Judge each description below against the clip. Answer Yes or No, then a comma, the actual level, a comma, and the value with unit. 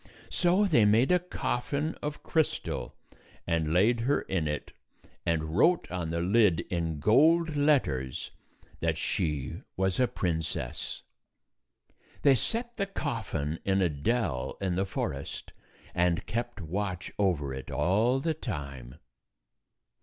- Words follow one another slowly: Yes, slow, 130 wpm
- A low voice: Yes, very low, 95 Hz